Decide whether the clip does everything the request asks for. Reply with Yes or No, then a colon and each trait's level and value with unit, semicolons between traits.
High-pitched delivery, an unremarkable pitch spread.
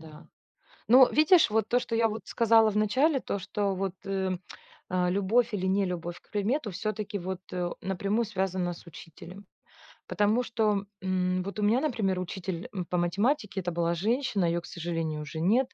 Yes: high, 195 Hz; average, 3.7 semitones